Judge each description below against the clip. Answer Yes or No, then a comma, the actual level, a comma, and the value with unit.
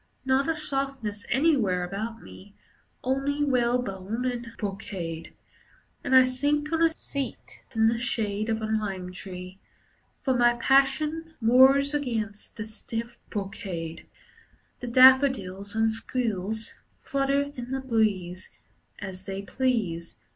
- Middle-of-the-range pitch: No, high, 230 Hz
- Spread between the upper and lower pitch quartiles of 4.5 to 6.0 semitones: Yes, average, 4.9 semitones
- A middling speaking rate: No, slow, 125 wpm